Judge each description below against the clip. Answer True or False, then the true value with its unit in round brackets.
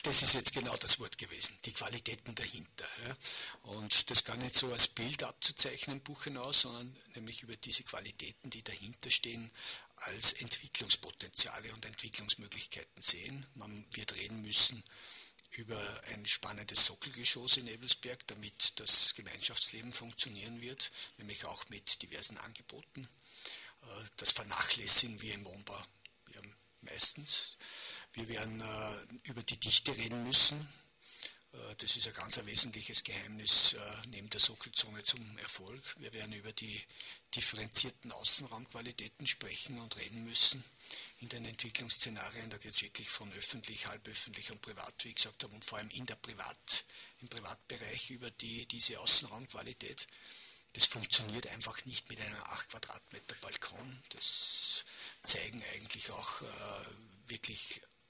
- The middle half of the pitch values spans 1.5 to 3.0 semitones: True (2.4 semitones)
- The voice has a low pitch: True (115 Hz)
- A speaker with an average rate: True (140 wpm)